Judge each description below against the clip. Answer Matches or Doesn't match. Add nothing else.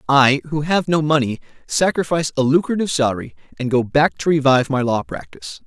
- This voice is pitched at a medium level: Matches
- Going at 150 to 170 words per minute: Doesn't match